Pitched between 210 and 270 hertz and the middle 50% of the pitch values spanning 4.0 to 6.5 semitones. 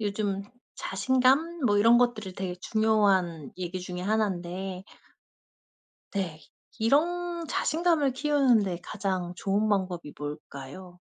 No: high, 200 Hz; wide, 5.5 semitones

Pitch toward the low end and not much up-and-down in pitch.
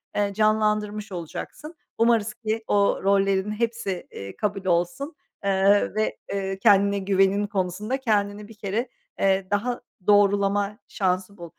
No: high, 205 Hz; narrow, 1.7 semitones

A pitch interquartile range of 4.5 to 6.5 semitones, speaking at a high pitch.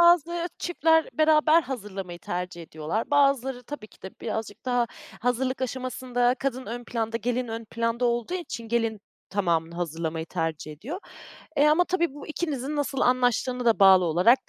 Yes: average, 5.3 semitones; high, 245 Hz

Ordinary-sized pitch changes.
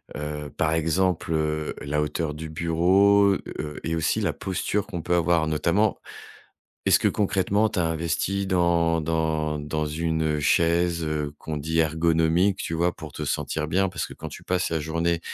No: narrow, 2.2 semitones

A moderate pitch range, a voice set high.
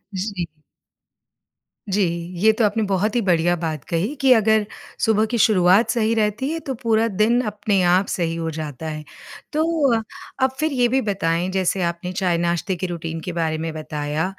Yes: average, 4.6 semitones; high, 195 Hz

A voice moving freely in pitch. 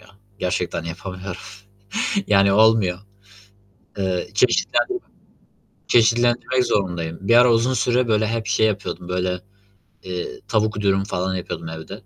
No: average, 3.9 semitones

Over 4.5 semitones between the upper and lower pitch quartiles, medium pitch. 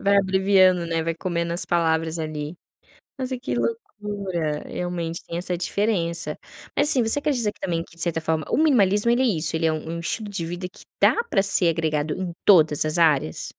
No: average, 3.8 semitones; medium, 175 Hz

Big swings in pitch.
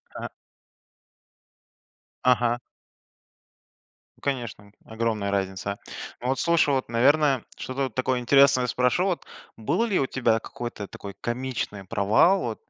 No: average, 3.8 semitones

